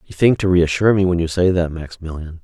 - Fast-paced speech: Yes, fast, 245 wpm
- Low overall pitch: Yes, very low, 85 Hz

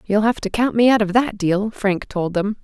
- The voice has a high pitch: Yes, high, 210 Hz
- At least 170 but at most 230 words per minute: No, fast, 275 wpm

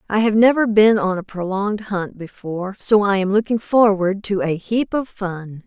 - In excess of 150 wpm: Yes, average, 200 wpm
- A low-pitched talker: No, high, 200 Hz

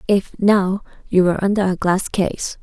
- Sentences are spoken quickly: No, average, 185 wpm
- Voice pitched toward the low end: No, high, 195 Hz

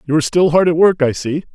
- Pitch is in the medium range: Yes, medium, 160 Hz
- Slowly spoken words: No, fast, 310 wpm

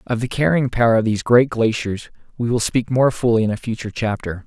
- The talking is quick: Yes, fast, 230 wpm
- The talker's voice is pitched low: Yes, low, 115 Hz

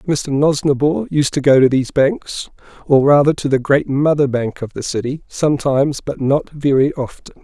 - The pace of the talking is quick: No, average, 185 wpm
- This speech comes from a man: Yes, male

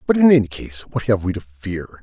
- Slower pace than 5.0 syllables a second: No, 5.3 syllables/s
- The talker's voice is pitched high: No, low, 105 Hz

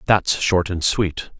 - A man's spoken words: Yes, male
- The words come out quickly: No, average, 170 wpm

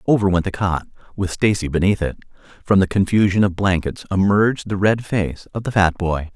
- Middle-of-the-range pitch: No, very low, 95 Hz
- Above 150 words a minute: Yes, average, 200 wpm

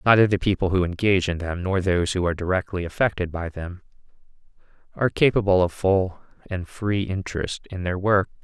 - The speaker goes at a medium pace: Yes, average, 180 wpm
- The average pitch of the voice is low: Yes, very low, 95 Hz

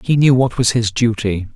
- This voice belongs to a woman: No, male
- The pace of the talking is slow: No, fast, 230 wpm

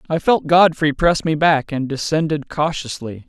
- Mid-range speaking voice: Yes, medium, 150 Hz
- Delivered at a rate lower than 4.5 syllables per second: No, 4.6 syllables/s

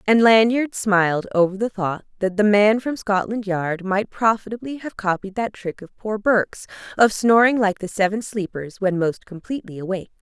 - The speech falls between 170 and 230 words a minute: Yes, average, 180 wpm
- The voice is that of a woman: Yes, female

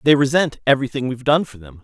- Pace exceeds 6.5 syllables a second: Yes, 7.1 syllables/s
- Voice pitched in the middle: No, low, 130 Hz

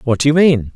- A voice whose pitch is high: No, low, 135 Hz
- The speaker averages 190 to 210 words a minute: No, fast, 320 wpm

